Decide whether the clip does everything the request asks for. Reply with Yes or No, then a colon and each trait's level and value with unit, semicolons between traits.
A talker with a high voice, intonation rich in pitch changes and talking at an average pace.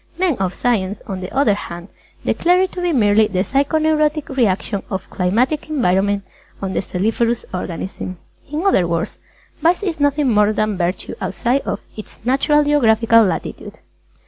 Yes: high, 225 Hz; wide, 7.4 semitones; average, 160 wpm